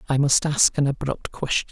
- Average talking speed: No, fast, 210 wpm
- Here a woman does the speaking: No, male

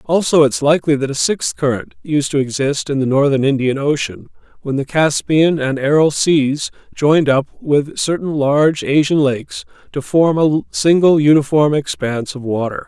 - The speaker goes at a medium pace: Yes, average, 170 wpm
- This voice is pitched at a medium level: Yes, medium, 145 Hz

